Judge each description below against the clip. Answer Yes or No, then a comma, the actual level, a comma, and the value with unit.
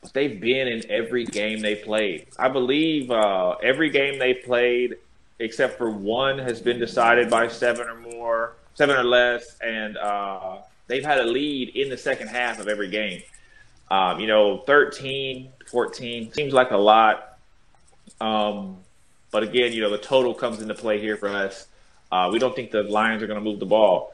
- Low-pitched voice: Yes, low, 115 Hz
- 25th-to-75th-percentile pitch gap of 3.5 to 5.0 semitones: No, average, 3.1 semitones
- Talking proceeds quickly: No, average, 185 wpm